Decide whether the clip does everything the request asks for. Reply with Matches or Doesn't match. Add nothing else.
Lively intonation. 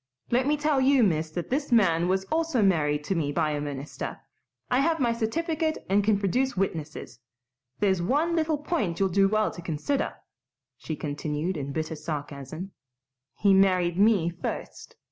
Matches